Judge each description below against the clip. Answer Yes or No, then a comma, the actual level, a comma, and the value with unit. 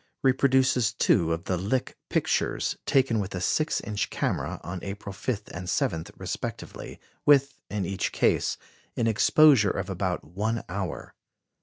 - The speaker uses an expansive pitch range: Yes, wide, 5.7 semitones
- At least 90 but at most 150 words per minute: Yes, average, 145 wpm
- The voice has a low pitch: Yes, low, 105 Hz